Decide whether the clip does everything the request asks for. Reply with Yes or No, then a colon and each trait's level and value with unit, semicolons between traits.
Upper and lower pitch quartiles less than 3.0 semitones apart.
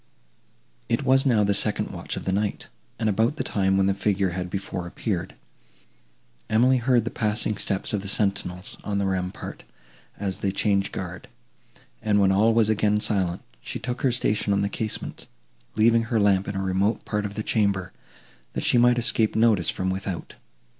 Yes: narrow, 2.5 semitones